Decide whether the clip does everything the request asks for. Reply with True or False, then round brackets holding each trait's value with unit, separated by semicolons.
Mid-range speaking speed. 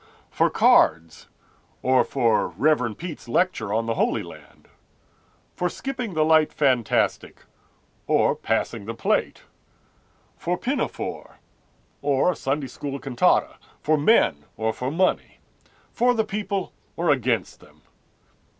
False (125 wpm)